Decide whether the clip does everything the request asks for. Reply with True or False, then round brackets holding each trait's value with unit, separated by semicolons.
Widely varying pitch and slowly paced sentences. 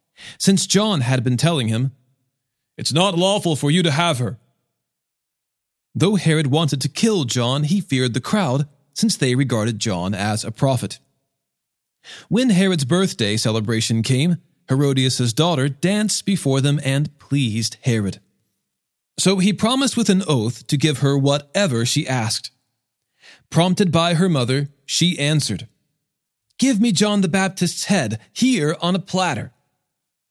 False (6.3 semitones; 145 wpm)